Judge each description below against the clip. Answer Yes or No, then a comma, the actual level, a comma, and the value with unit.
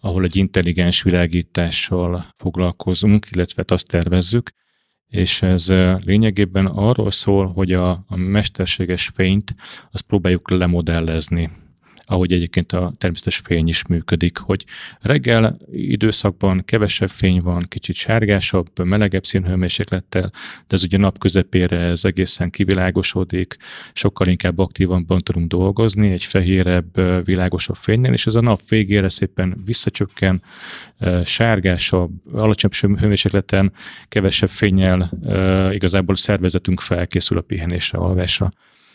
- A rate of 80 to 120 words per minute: Yes, average, 110 wpm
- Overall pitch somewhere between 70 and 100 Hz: Yes, very low, 95 Hz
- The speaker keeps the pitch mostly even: Yes, narrow, 2.1 semitones